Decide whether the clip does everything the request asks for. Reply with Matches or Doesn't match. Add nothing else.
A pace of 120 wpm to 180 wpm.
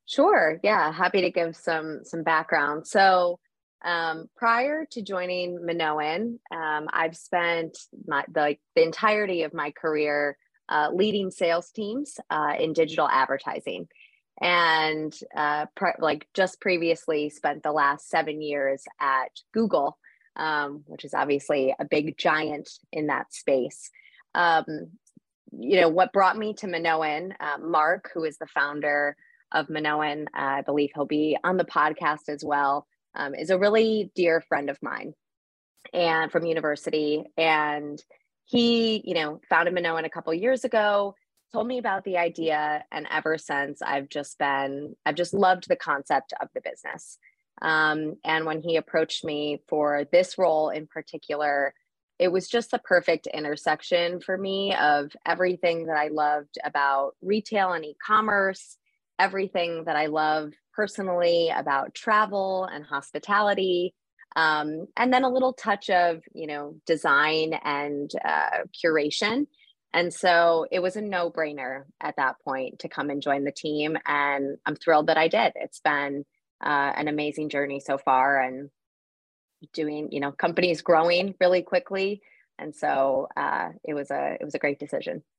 Matches